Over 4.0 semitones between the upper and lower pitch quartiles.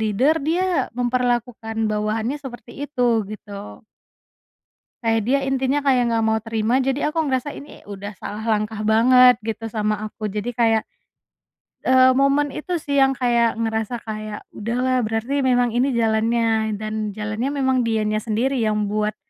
No: average, 3.2 semitones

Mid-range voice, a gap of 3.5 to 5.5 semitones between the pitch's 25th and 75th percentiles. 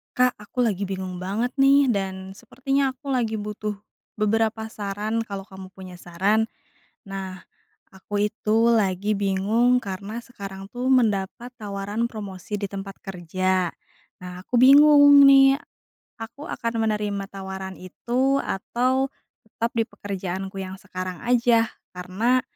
No: high, 210 Hz; average, 3.9 semitones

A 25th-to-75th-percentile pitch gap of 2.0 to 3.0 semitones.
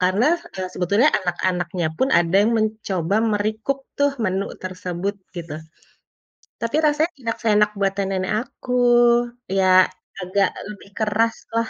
No: average, 3.6 semitones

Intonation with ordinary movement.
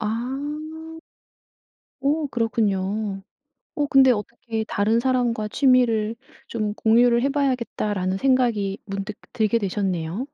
Yes: average, 3.8 semitones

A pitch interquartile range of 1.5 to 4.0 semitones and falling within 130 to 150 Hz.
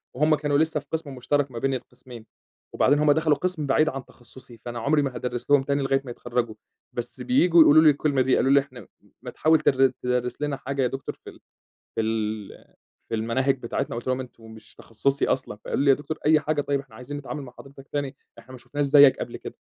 Yes: average, 2.9 semitones; low, 135 Hz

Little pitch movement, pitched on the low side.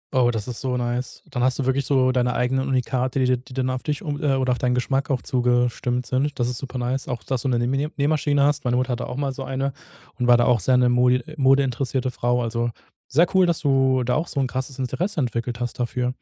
Yes: narrow, 1.6 semitones; low, 130 Hz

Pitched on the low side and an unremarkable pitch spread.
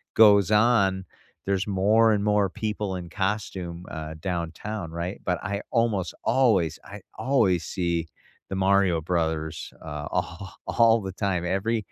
Yes: very low, 95 Hz; average, 3.4 semitones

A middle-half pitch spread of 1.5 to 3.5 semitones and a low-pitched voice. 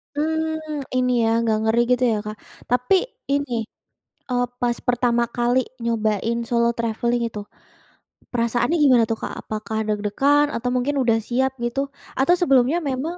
No: average, 2.9 semitones; high, 245 Hz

